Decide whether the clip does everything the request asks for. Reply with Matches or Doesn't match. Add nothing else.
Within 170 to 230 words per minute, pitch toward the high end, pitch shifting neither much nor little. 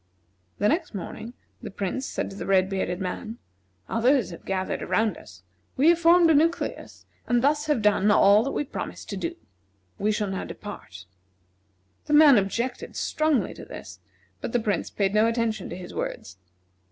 Doesn't match